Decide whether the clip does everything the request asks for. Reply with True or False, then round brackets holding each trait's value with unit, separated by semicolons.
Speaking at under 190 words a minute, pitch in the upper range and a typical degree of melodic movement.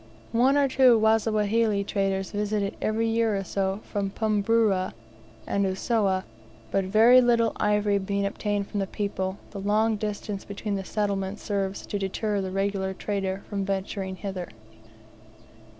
False (150 wpm; 200 Hz; 1.9 semitones)